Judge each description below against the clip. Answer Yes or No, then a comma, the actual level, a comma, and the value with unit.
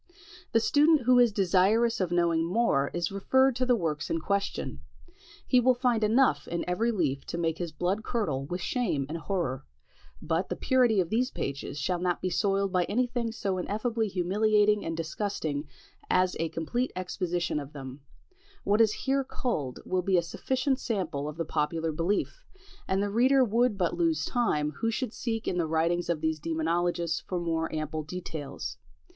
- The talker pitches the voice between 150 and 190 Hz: Yes, medium, 185 Hz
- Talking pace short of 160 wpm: No, average, 180 wpm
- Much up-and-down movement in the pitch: Yes, wide, 5.8 semitones